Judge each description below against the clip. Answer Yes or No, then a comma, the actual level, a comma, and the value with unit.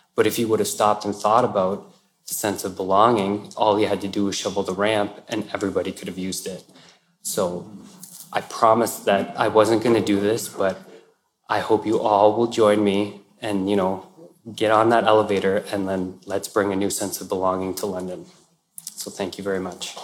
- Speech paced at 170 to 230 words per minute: Yes, fast, 205 wpm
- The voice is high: No, low, 100 Hz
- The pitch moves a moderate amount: No, narrow, 1.7 semitones